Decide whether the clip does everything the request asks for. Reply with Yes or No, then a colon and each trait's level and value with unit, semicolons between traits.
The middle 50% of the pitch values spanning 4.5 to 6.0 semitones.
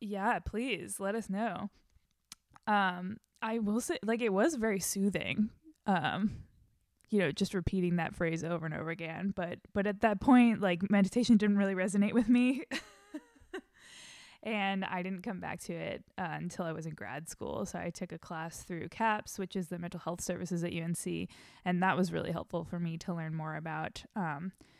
No: average, 3.8 semitones